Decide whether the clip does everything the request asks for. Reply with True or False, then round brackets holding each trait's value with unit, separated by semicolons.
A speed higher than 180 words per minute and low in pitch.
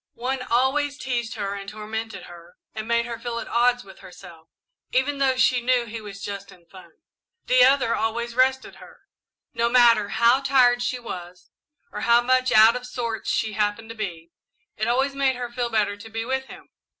False (195 wpm; 235 Hz)